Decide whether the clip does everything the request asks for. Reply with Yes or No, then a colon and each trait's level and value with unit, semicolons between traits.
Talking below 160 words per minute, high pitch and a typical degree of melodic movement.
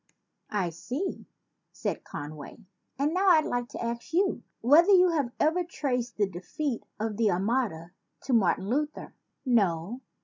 No: average, 150 wpm; high, 240 Hz; wide, 7.5 semitones